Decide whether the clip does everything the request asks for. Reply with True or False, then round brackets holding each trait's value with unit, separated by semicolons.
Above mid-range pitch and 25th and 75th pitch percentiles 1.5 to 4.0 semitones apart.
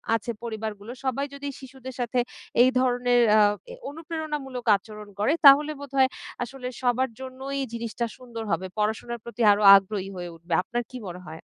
True (245 Hz; 3.6 semitones)